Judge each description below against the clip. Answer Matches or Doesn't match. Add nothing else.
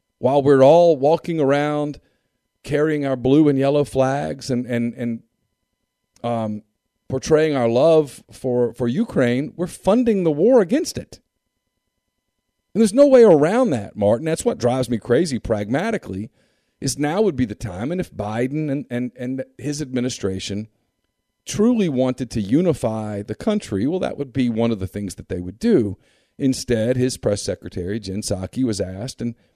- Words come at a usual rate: Matches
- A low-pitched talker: Matches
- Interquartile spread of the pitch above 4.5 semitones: Matches